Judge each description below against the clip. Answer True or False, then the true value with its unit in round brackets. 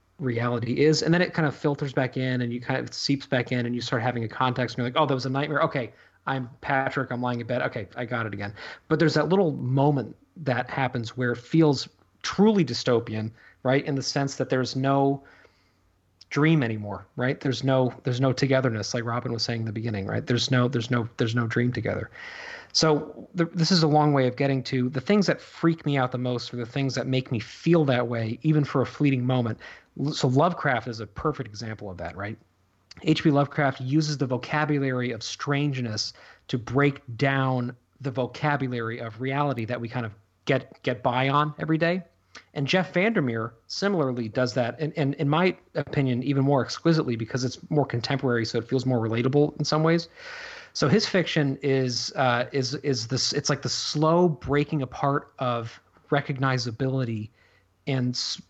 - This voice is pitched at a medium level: False (130 Hz)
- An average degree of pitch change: True (3.4 semitones)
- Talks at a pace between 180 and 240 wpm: True (200 wpm)